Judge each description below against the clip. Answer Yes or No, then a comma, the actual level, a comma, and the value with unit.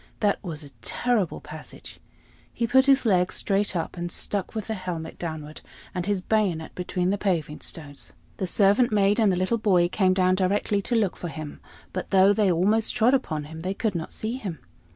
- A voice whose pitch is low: No, high, 190 Hz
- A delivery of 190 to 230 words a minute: Yes, average, 195 wpm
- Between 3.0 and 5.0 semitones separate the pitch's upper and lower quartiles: Yes, average, 3.6 semitones